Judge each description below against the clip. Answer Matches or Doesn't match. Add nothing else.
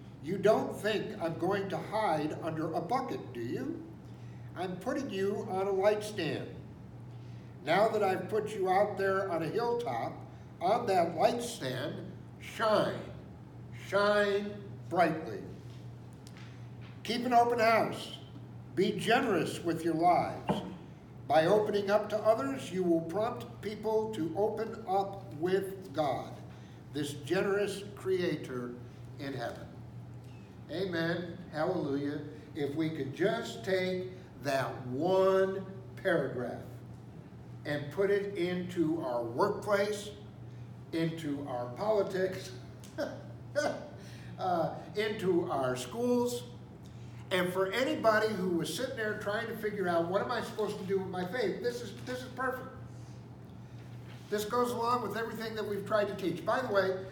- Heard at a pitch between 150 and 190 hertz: Matches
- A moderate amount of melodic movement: Doesn't match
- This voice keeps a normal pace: Doesn't match